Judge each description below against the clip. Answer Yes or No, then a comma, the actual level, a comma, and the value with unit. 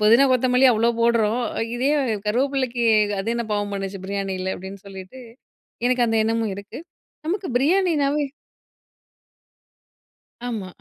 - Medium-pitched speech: No, high, 230 Hz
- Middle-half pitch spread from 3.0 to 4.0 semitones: No, average, 4.5 semitones